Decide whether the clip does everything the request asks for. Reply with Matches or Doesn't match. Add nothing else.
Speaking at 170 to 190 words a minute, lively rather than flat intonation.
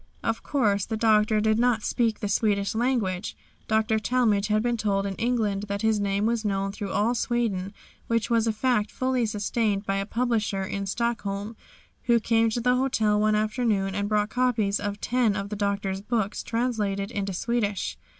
Doesn't match